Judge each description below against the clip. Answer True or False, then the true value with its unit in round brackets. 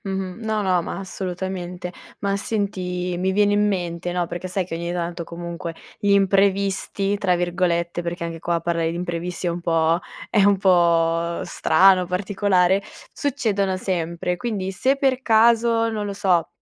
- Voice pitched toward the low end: False (185 Hz)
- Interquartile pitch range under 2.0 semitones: False (2.5 semitones)